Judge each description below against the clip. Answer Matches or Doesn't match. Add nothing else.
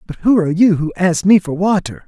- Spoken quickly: Matches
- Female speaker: Doesn't match